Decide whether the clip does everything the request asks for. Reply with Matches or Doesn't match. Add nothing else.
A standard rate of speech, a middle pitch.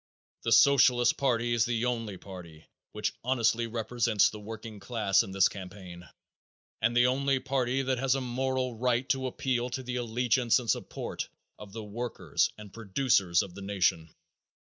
Doesn't match